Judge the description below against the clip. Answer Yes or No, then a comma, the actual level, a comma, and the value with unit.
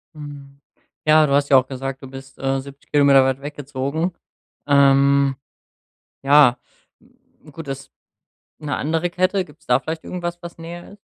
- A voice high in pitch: No, medium, 140 Hz